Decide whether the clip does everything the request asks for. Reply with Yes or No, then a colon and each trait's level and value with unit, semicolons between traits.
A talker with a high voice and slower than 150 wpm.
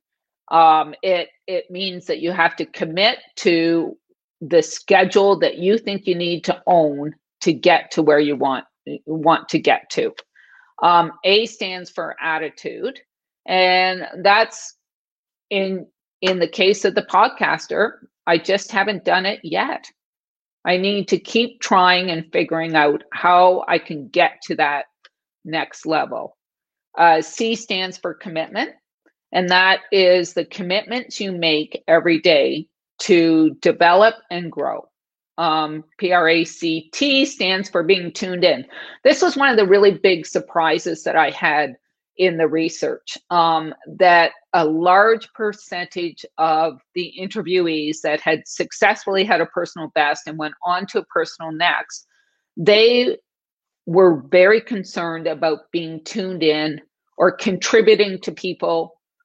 No: medium, 180 Hz; average, 140 wpm